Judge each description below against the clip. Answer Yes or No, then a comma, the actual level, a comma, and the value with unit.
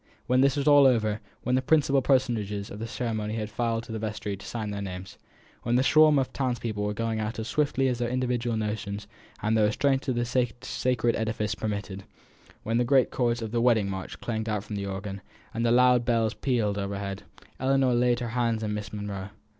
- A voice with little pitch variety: No, average, 3.0 semitones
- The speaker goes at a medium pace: No, fast, 210 wpm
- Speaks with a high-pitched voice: No, low, 115 Hz